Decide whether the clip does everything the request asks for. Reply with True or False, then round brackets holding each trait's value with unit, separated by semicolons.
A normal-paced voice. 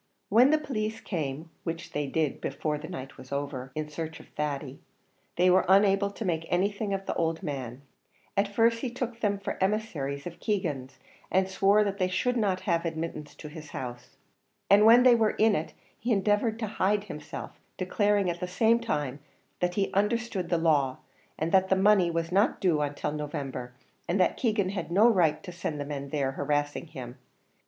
True (195 wpm)